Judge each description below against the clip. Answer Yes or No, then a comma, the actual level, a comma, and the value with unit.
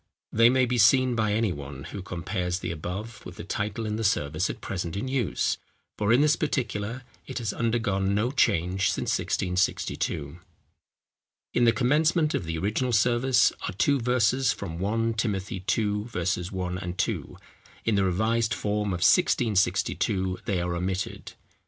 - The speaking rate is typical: Yes, average, 160 wpm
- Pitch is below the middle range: Yes, low, 105 Hz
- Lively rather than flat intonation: No, average, 4.5 semitones